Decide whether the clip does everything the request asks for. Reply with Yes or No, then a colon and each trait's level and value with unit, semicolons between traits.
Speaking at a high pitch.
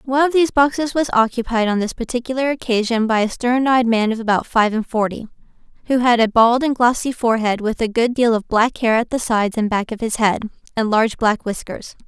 Yes: high, 235 Hz